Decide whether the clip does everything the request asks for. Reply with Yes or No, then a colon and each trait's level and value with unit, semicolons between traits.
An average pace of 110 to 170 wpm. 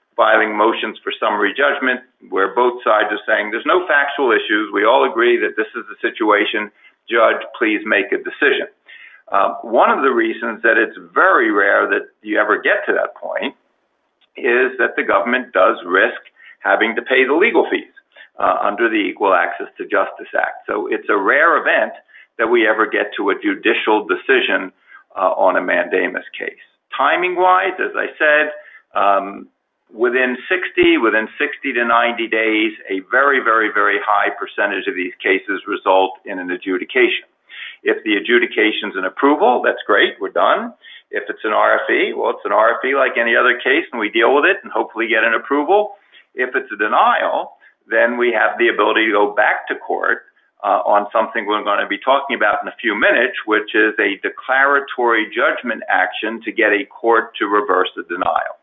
No: average, 185 wpm